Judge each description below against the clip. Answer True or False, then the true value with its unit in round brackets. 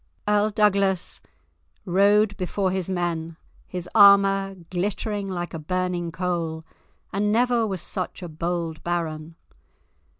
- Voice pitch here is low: False (185 Hz)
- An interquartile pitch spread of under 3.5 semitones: True (2.7 semitones)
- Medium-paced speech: False (120 wpm)